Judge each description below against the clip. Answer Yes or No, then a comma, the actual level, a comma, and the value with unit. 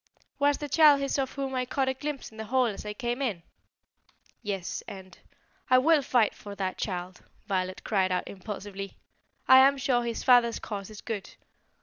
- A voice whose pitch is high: Yes, high, 235 Hz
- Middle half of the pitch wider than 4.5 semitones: Yes, average, 5.1 semitones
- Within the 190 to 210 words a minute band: Yes, average, 195 wpm